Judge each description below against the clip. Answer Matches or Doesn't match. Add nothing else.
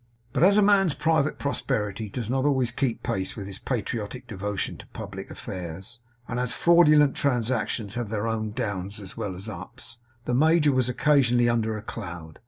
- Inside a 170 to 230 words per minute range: Matches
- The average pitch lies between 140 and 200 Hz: Doesn't match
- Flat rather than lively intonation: Doesn't match